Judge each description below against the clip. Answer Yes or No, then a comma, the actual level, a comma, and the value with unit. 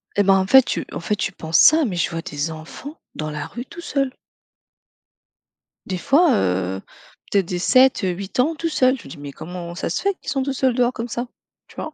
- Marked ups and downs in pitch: Yes, wide, 7.8 semitones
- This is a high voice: Yes, high, 200 Hz